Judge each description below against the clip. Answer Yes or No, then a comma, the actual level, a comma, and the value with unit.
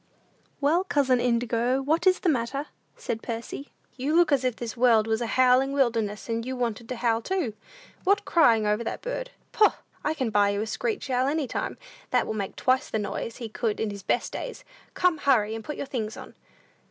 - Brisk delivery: Yes, fast, 210 wpm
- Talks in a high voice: Yes, high, 245 Hz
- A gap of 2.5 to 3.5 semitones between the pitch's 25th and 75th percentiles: No, average, 4.2 semitones